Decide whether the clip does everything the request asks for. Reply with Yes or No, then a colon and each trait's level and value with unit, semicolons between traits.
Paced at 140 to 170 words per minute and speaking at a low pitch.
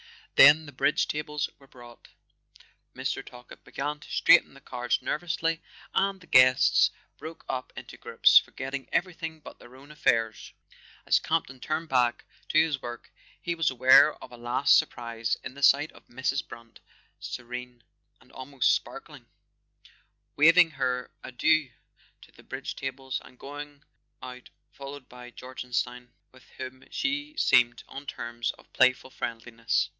Yes: average, 145 wpm; low, 130 Hz